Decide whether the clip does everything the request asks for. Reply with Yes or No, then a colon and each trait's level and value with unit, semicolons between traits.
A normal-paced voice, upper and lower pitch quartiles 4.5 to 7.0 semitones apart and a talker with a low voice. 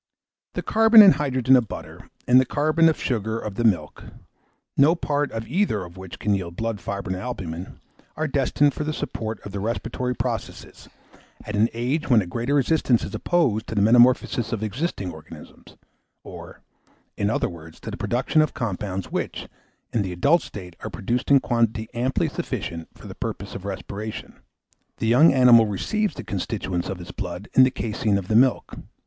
Yes: average, 185 wpm; average, 5.2 semitones; low, 115 Hz